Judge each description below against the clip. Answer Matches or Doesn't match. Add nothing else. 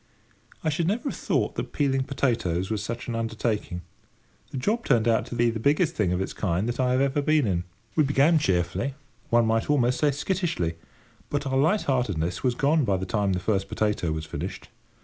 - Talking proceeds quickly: Matches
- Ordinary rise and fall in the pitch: Doesn't match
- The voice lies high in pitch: Doesn't match